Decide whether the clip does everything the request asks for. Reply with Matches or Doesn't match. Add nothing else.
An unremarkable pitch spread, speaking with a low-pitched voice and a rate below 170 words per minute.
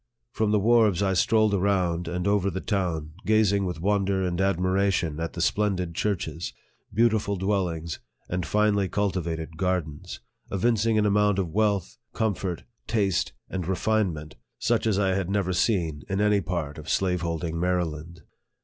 Matches